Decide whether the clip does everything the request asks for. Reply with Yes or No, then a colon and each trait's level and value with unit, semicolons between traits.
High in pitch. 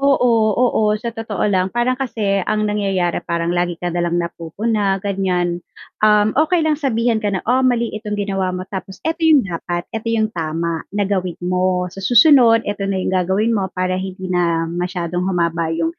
Yes: high, 195 Hz